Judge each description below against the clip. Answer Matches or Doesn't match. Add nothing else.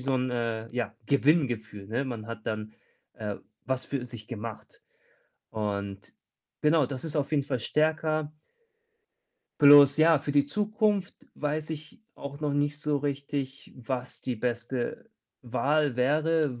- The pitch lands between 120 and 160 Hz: Matches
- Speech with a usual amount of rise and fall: Matches